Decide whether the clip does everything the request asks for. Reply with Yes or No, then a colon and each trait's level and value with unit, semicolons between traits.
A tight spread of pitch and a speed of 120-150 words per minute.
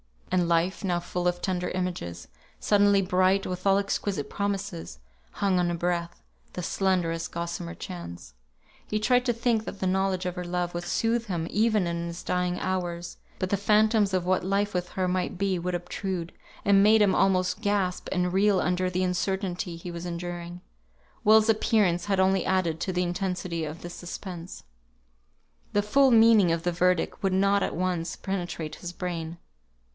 No: narrow, 2.2 semitones; average, 175 wpm